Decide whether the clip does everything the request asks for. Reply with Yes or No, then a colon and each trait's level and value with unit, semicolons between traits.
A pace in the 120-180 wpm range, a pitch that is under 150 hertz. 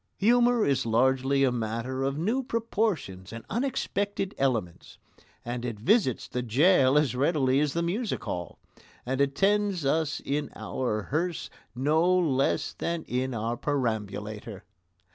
Yes: slow, 135 wpm; low, 135 Hz